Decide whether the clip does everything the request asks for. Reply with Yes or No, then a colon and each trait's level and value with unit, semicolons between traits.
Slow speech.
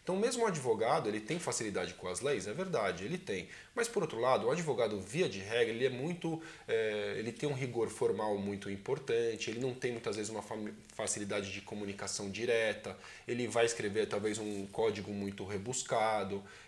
No: fast, 185 wpm